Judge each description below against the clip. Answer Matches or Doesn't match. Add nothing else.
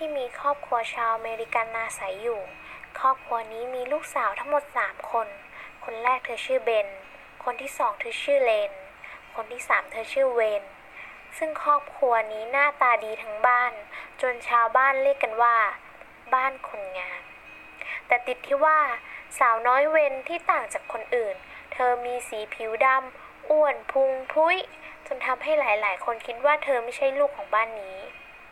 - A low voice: Doesn't match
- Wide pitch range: Doesn't match